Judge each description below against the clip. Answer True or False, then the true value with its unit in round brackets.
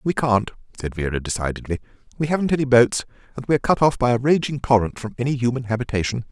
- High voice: False (125 Hz)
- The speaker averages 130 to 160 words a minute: False (200 wpm)